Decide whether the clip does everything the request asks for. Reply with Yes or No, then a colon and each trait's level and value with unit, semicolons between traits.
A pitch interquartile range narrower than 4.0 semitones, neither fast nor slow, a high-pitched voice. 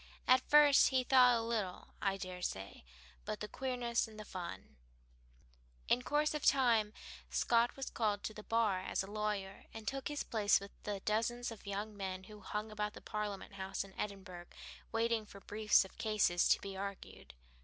Yes: average, 3.1 semitones; average, 185 wpm; high, 210 Hz